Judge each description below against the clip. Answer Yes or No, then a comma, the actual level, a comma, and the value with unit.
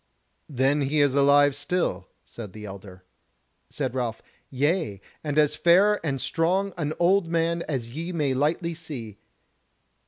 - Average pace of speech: Yes, average, 145 wpm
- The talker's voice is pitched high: No, medium, 145 Hz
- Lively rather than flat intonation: No, average, 4.7 semitones